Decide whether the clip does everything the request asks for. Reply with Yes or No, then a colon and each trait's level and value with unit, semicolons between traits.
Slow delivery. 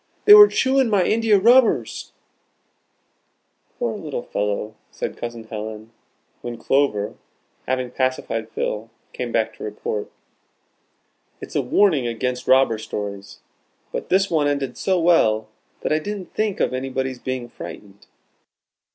Yes: slow, 130 wpm